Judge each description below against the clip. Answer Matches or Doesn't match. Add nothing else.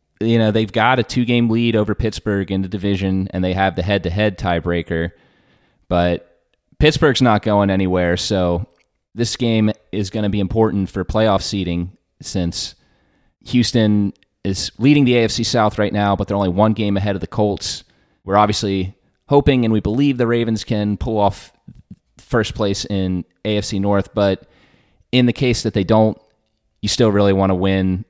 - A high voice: Doesn't match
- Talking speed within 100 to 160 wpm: Doesn't match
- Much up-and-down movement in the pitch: Doesn't match